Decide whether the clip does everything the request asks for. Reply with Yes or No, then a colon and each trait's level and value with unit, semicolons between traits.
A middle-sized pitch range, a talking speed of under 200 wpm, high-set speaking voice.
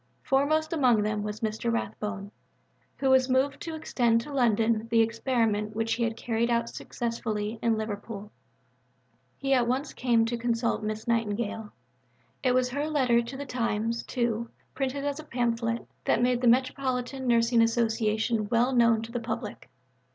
No: narrow, 2.3 semitones; average, 160 wpm; high, 235 Hz